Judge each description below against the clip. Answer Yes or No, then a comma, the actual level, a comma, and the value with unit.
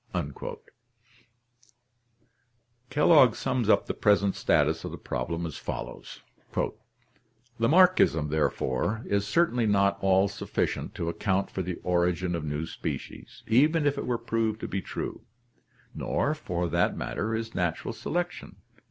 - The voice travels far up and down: Yes, wide, 5.7 semitones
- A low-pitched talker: Yes, low, 100 Hz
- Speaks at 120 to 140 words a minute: Yes, slow, 135 wpm